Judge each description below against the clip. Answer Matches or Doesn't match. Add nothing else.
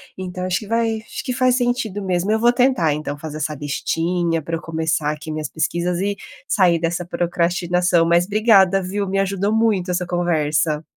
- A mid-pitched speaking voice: Matches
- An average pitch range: Matches